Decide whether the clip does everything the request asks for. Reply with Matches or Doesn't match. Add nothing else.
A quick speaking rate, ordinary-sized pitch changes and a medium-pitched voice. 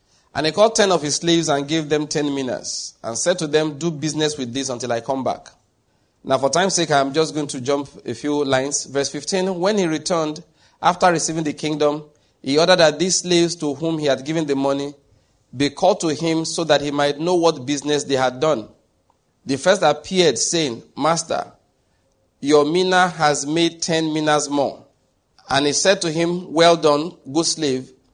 Doesn't match